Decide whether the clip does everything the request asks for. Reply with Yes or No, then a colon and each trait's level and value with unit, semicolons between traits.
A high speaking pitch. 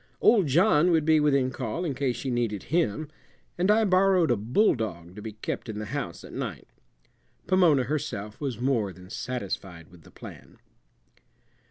No: low, 130 Hz